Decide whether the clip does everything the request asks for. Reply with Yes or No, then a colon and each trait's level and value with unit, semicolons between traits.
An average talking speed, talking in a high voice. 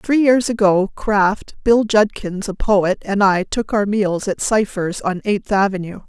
Yes: average, 180 wpm; high, 205 Hz